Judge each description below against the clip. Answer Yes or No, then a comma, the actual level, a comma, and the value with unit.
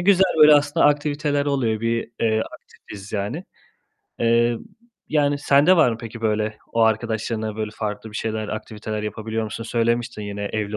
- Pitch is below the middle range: Yes, low, 115 Hz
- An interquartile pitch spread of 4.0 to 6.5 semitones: Yes, average, 4.7 semitones